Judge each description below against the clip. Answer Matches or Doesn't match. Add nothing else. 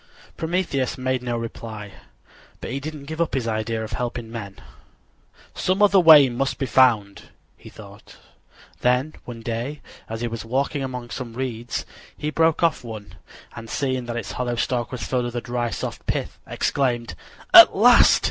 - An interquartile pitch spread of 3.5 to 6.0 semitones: Doesn't match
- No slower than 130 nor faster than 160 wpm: Doesn't match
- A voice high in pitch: Doesn't match